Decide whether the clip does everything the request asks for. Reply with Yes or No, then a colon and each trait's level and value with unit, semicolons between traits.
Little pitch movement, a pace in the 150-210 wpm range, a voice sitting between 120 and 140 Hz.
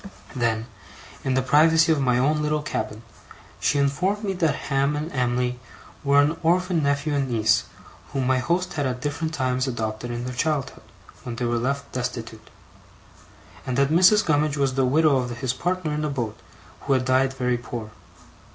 No: average, 3.4 semitones; average, 180 wpm; low, 135 Hz